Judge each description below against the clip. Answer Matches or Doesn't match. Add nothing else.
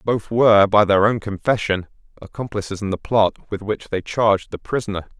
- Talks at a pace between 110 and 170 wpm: Doesn't match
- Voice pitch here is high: Doesn't match